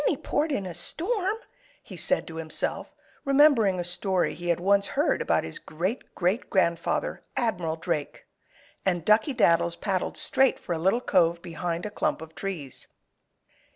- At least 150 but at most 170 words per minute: Yes, average, 160 wpm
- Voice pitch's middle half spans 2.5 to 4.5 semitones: No, average, 5.3 semitones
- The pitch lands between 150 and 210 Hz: Yes, medium, 185 Hz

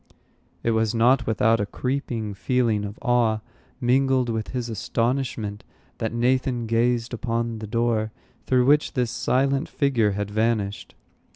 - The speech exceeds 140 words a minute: No, slow, 135 wpm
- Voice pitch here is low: Yes, low, 115 Hz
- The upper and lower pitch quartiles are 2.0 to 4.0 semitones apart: Yes, narrow, 2.5 semitones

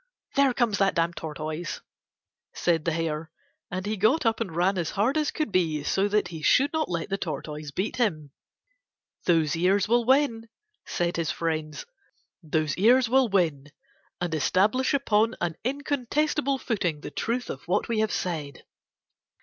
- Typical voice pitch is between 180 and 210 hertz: Yes, high, 190 Hz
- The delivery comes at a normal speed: Yes, average, 165 wpm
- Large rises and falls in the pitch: Yes, wide, 6.6 semitones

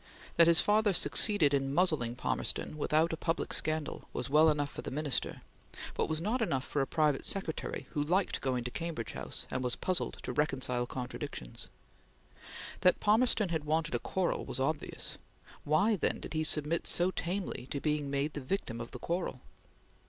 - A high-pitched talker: No, medium, 155 Hz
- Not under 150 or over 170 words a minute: No, average, 180 wpm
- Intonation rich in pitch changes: No, average, 4.1 semitones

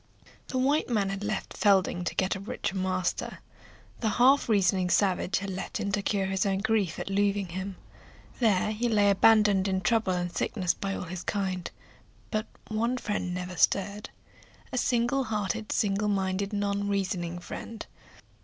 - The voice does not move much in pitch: Yes, narrow, 2.3 semitones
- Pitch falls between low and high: No, high, 200 Hz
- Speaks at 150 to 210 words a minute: Yes, average, 165 wpm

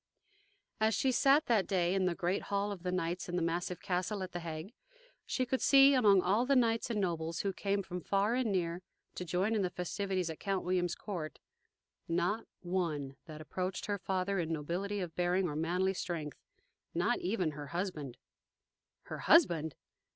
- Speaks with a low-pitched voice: No, medium, 185 Hz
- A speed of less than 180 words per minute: No, average, 185 wpm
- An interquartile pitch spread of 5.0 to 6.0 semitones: No, average, 2.9 semitones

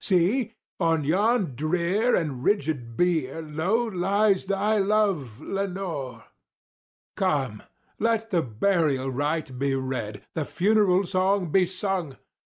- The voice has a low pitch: No, medium, 175 Hz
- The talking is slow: Yes, slow, 110 wpm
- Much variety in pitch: Yes, wide, 5.9 semitones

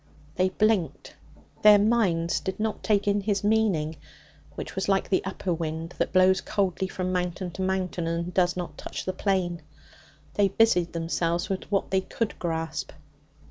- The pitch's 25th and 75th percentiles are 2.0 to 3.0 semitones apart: Yes, narrow, 2.6 semitones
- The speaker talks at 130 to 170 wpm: Yes, average, 165 wpm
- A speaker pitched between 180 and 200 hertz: Yes, medium, 185 Hz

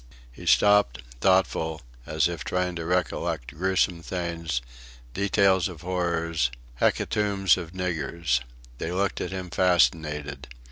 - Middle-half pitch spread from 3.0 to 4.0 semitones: No, narrow, 2.6 semitones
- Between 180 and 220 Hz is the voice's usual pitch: No, very low, 85 Hz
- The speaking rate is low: Yes, slow, 120 wpm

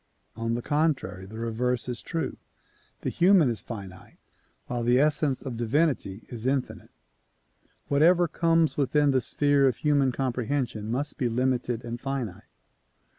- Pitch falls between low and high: No, low, 130 Hz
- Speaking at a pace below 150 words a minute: Yes, average, 140 wpm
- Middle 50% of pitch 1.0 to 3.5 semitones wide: No, average, 3.9 semitones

